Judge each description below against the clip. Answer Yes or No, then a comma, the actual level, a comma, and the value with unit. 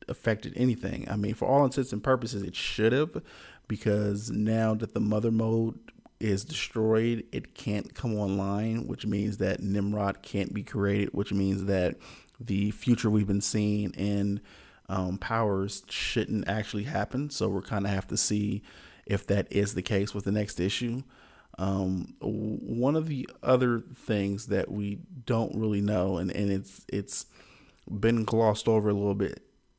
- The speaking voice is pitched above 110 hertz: No, low, 105 Hz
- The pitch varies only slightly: Yes, narrow, 2.3 semitones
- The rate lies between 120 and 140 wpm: No, average, 165 wpm